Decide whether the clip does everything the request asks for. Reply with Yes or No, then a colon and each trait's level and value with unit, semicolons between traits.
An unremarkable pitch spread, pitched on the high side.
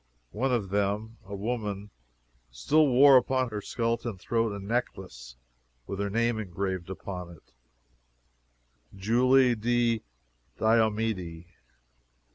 No: average, 3.6 semitones; low, 110 Hz